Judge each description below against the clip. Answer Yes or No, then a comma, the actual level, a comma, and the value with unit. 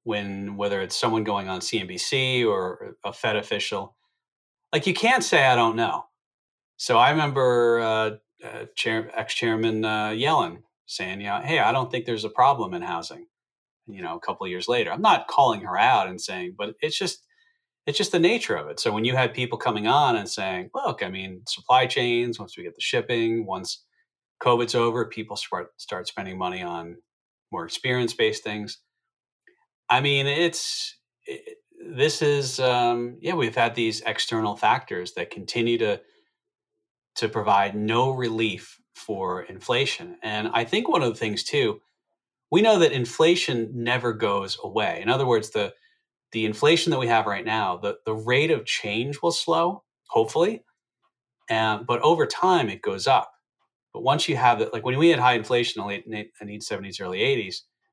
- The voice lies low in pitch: Yes, low, 120 Hz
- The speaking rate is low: No, average, 185 wpm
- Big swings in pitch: Yes, wide, 8.0 semitones